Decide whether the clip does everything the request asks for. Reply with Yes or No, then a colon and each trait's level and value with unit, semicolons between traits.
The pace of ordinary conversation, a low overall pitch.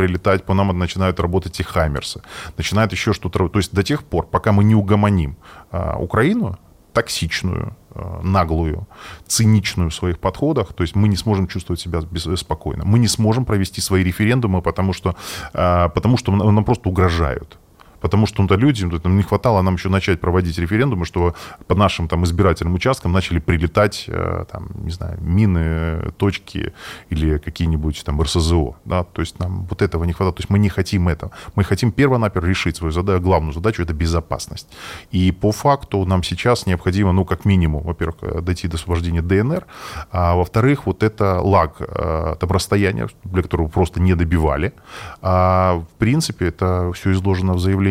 No: fast, 175 wpm; very low, 95 Hz